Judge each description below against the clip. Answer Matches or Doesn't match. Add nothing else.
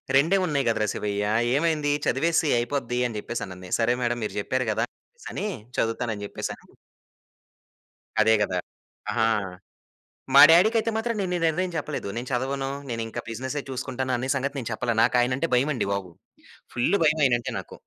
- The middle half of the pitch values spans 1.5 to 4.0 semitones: Doesn't match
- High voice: Doesn't match